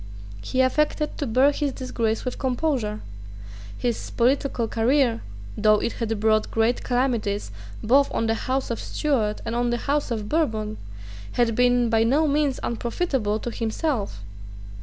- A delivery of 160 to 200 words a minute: No, average, 150 wpm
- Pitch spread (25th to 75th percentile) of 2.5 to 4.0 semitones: Yes, average, 3.4 semitones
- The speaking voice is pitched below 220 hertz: No, high, 240 Hz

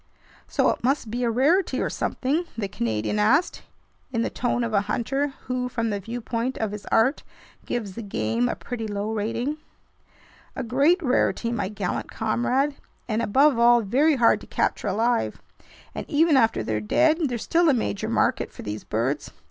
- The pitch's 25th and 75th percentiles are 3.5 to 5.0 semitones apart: Yes, average, 4.2 semitones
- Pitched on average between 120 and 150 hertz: No, high, 235 Hz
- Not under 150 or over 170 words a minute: No, average, 180 wpm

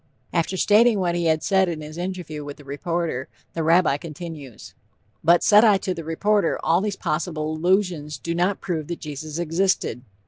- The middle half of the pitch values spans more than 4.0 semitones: No, average, 3.2 semitones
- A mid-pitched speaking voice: Yes, medium, 170 Hz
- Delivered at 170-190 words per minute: Yes, average, 185 wpm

